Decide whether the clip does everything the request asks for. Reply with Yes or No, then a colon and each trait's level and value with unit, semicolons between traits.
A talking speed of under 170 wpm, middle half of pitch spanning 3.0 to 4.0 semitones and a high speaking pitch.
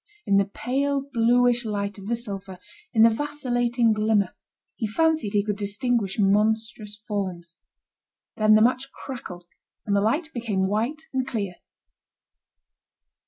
Yes: slow, 135 wpm; average, 3.4 semitones; high, 220 Hz